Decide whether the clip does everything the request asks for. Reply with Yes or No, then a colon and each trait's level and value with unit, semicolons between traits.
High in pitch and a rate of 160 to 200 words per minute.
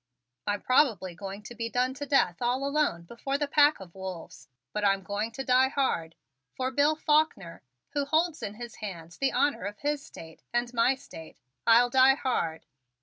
Yes: high, 245 Hz; average, 185 wpm